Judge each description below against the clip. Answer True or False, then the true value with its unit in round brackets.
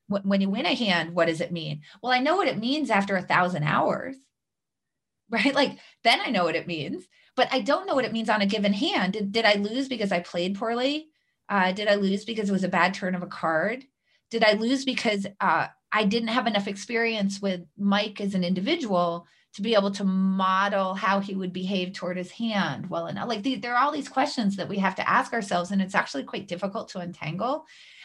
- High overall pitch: True (200 Hz)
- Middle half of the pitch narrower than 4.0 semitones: False (4.4 semitones)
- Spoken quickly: True (230 wpm)